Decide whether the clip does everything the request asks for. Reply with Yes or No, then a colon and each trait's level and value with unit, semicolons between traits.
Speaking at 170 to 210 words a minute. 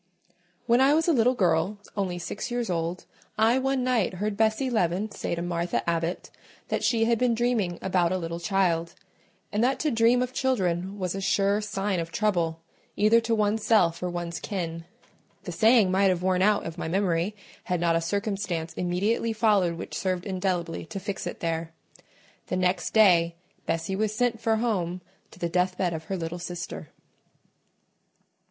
Yes: average, 180 wpm